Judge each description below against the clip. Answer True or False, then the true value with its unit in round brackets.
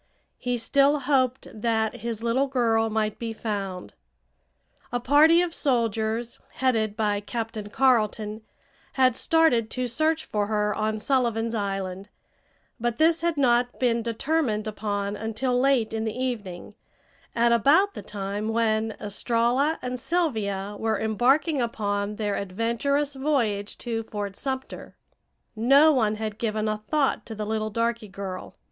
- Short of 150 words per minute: True (140 wpm)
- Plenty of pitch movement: False (3.4 semitones)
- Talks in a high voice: True (230 Hz)